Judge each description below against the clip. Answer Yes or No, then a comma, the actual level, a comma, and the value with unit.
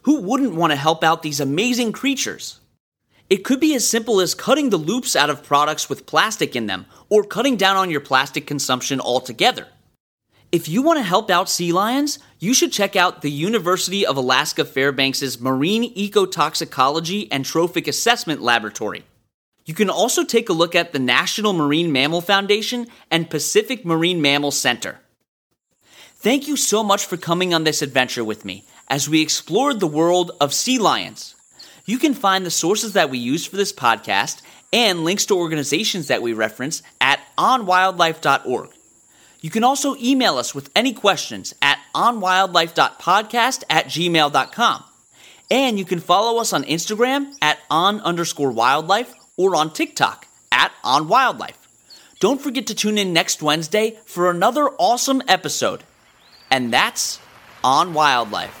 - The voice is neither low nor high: Yes, medium, 175 Hz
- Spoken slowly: No, average, 155 wpm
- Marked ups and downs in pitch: Yes, wide, 7.1 semitones